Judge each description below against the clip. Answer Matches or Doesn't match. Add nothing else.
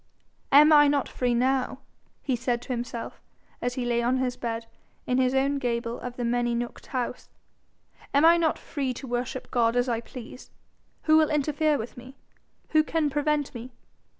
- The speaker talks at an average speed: Matches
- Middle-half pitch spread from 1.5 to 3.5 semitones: Matches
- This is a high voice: Matches